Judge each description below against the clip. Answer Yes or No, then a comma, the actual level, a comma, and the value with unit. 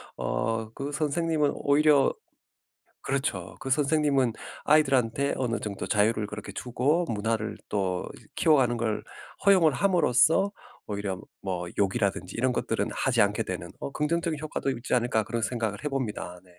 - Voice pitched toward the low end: Yes, low, 125 Hz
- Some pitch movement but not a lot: No, wide, 5.7 semitones